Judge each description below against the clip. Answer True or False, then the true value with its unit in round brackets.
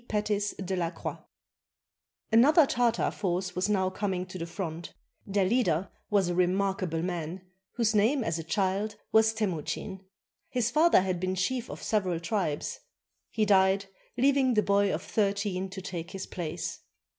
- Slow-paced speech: False (155 wpm)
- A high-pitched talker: True (195 Hz)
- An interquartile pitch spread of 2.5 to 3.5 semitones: True (3.0 semitones)